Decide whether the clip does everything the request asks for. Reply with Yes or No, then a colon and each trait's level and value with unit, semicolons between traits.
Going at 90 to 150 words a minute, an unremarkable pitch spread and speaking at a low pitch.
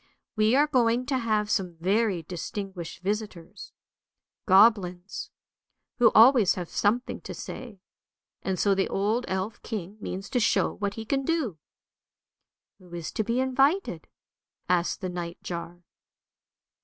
No: average, 145 wpm; average, 4.3 semitones; high, 205 Hz